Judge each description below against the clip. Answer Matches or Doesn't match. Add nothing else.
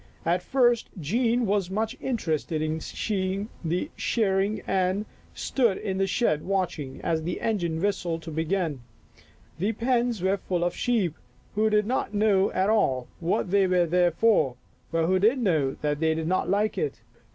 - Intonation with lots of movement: Doesn't match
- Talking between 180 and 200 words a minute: Doesn't match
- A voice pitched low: Doesn't match